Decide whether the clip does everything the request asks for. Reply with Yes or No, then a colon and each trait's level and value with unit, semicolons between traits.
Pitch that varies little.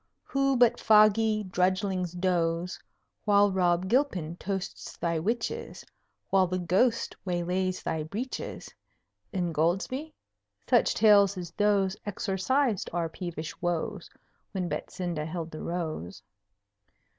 No: average, 3.3 semitones